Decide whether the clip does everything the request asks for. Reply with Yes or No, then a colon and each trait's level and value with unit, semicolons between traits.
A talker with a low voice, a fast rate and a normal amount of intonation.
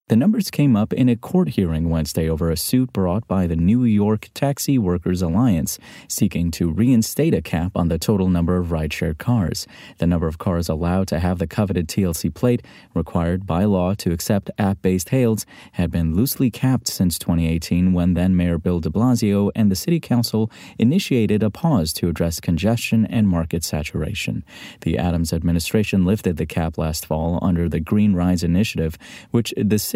No: very low, 90 Hz; average, 185 wpm; average, 4.4 semitones